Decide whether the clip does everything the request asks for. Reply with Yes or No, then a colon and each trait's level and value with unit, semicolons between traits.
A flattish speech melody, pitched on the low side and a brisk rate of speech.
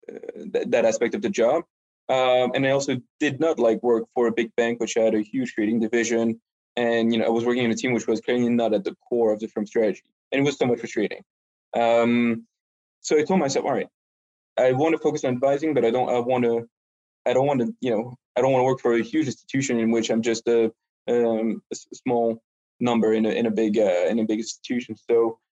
Yes: narrow, 2.1 semitones; low, 115 Hz; fast, 245 wpm